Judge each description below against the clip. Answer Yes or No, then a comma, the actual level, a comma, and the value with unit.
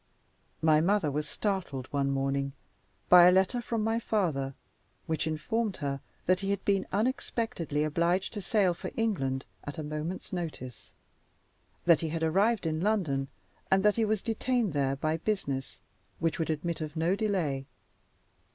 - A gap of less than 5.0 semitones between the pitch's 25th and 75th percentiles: No, wide, 5.5 semitones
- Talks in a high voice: No, medium, 170 Hz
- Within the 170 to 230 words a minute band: No, average, 160 wpm